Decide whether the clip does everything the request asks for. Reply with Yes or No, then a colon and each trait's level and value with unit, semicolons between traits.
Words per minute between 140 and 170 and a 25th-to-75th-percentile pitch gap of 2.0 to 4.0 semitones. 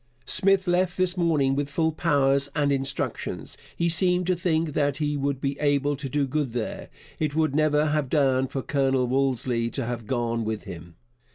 No: average, 185 wpm; average, 3.0 semitones